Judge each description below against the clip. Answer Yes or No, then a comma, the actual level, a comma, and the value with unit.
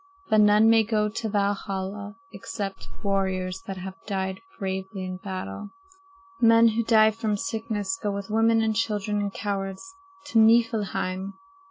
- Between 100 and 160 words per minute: Yes, average, 145 wpm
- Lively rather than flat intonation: No, narrow, 2.5 semitones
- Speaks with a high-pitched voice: Yes, high, 205 Hz